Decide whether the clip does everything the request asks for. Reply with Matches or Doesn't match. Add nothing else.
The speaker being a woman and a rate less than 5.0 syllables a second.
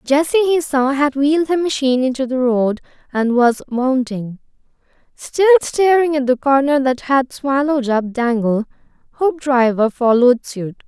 Matches